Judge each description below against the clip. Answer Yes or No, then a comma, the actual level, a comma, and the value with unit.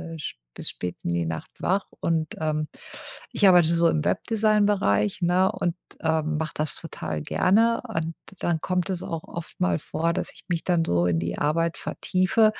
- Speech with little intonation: No, average, 3.3 semitones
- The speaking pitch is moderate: Yes, medium, 165 Hz